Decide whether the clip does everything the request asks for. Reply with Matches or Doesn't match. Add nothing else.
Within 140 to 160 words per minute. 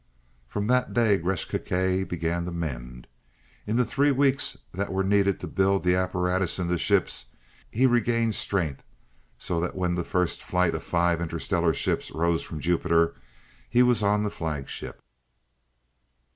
Matches